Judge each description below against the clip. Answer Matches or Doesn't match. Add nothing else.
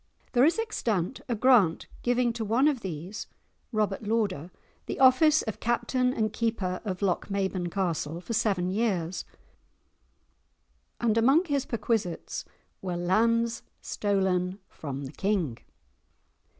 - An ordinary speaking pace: Doesn't match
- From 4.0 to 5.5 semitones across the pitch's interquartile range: Matches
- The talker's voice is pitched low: Doesn't match